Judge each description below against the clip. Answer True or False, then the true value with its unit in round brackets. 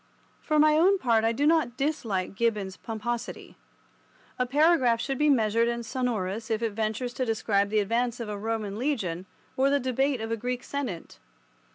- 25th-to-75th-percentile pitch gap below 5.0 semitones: True (3.7 semitones)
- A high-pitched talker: True (235 Hz)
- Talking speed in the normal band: True (180 wpm)